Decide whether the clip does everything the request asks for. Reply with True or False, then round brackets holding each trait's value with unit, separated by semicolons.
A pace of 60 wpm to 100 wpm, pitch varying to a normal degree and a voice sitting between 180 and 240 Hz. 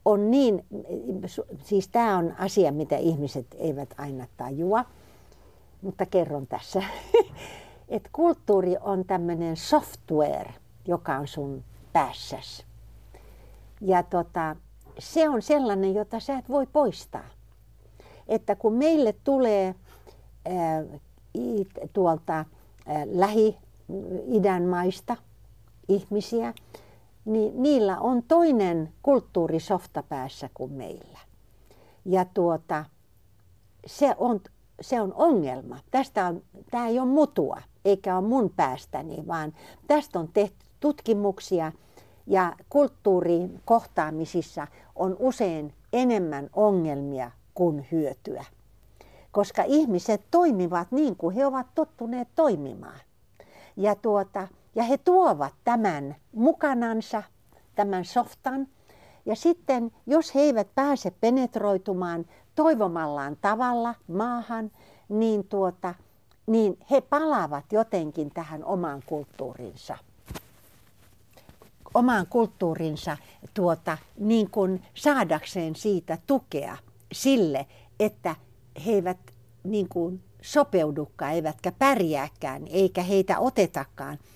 False (95 wpm; 6.7 semitones; 190 Hz)